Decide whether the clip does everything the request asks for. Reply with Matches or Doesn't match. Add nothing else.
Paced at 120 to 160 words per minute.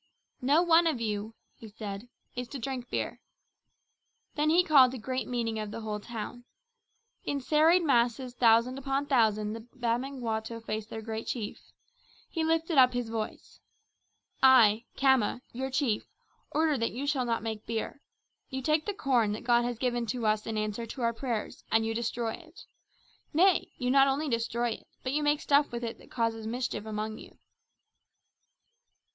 Doesn't match